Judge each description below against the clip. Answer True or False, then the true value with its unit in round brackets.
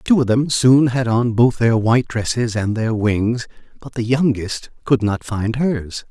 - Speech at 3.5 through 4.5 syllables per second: True (4.2 syllables/s)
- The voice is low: True (120 Hz)